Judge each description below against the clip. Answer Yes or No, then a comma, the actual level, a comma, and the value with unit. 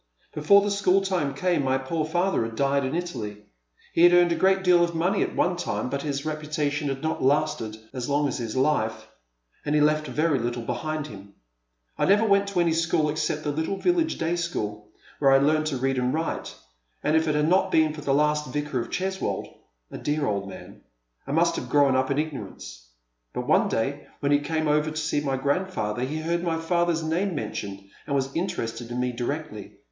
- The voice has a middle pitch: Yes, medium, 150 Hz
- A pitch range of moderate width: Yes, average, 4.1 semitones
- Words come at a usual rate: No, fast, 215 wpm